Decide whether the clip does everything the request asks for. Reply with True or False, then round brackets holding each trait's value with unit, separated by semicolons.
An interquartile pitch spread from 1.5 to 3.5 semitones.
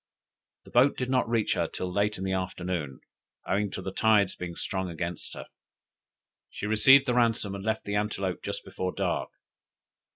True (3.2 semitones)